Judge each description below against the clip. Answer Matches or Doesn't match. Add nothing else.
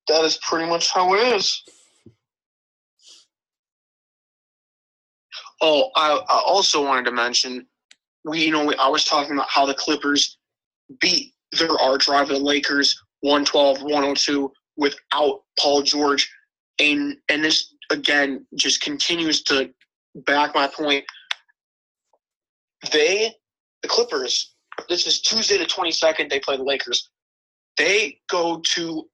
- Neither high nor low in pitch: Matches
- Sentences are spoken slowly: Matches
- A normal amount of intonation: Matches